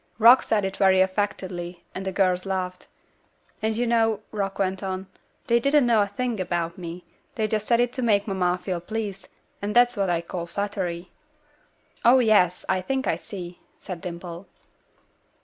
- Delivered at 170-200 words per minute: Yes, average, 180 wpm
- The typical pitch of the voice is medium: No, high, 195 Hz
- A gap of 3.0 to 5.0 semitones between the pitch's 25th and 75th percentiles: Yes, average, 3.4 semitones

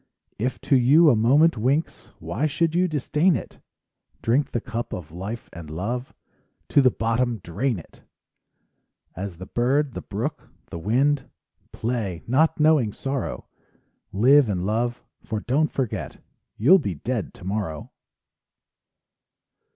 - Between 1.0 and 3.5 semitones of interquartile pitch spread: No, wide, 5.5 semitones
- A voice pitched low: Yes, low, 120 Hz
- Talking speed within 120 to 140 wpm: Yes, slow, 135 wpm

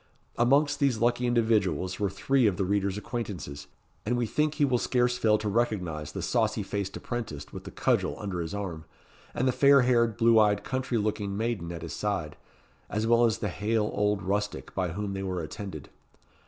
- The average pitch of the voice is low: Yes, low, 105 Hz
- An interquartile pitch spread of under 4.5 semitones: Yes, average, 3.9 semitones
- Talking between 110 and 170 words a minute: No, average, 195 wpm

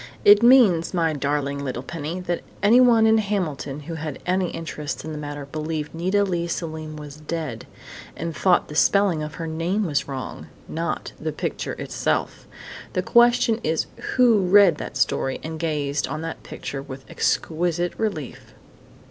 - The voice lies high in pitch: No, medium, 165 Hz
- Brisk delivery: No, average, 160 wpm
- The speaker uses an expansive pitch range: No, average, 3.9 semitones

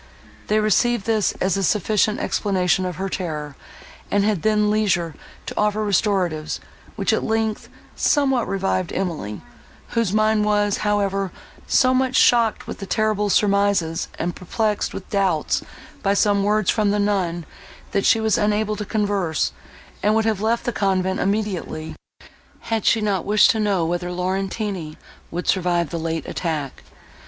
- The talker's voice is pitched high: Yes, high, 200 Hz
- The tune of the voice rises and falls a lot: No, average, 2.9 semitones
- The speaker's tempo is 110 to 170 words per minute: Yes, average, 155 wpm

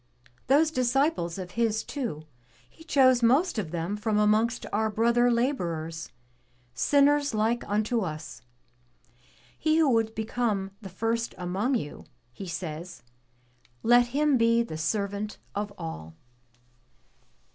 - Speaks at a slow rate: Yes, slow, 125 wpm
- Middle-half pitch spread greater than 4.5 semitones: Yes, average, 5.0 semitones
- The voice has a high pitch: Yes, high, 220 Hz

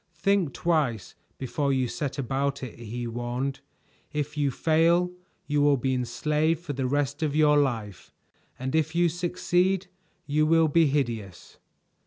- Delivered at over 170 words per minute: No, average, 150 wpm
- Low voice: No, medium, 145 Hz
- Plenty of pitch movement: No, average, 3.6 semitones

